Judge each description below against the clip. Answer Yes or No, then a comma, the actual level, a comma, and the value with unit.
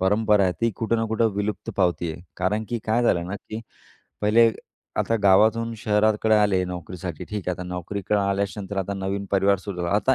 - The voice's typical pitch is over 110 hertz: No, low, 100 Hz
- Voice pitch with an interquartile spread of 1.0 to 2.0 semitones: No, average, 2.7 semitones